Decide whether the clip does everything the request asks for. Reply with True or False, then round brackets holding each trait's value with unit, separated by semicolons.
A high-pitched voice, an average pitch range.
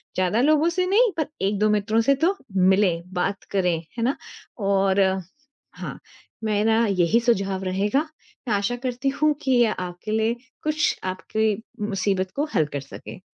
True (210 Hz; 4.4 semitones)